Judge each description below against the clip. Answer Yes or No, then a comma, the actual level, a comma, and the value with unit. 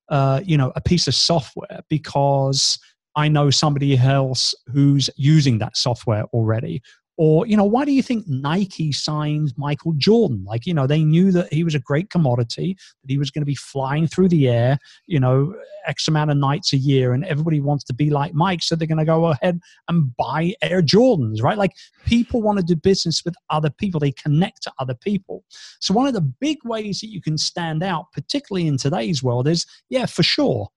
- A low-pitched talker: No, medium, 155 Hz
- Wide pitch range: No, average, 4.3 semitones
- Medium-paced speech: No, fast, 210 wpm